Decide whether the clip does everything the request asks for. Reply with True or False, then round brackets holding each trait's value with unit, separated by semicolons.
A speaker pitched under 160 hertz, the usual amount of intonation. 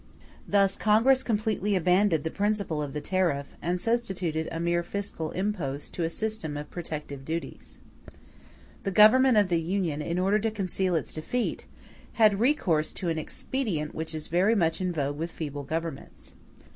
False (180 Hz; 4.7 semitones)